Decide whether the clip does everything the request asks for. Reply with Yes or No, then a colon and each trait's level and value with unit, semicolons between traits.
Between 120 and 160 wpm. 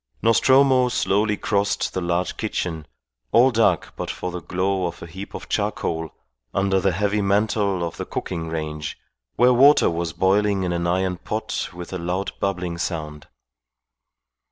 Yes: average, 155 wpm